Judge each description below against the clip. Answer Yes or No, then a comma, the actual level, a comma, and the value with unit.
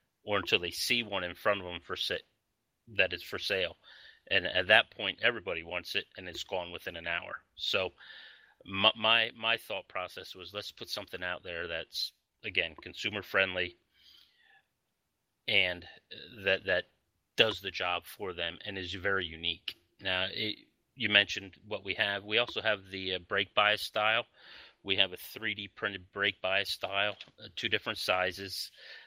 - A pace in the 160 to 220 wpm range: Yes, average, 165 wpm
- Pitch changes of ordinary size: No, narrow, 2.2 semitones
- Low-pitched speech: Yes, very low, 95 Hz